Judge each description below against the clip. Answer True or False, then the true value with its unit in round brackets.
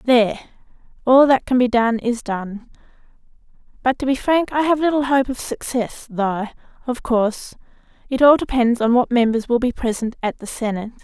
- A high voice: True (240 Hz)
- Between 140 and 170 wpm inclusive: False (180 wpm)